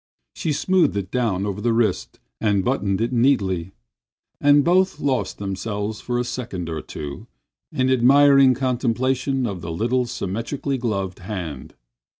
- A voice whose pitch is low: Yes, low, 115 Hz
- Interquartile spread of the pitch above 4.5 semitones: Yes, average, 5.1 semitones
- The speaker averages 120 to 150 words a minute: Yes, average, 145 wpm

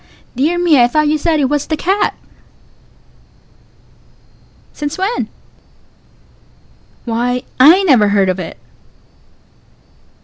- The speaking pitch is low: No, very high, 295 Hz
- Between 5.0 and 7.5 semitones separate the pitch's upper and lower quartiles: Yes, wide, 5.5 semitones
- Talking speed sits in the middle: No, slow, 125 wpm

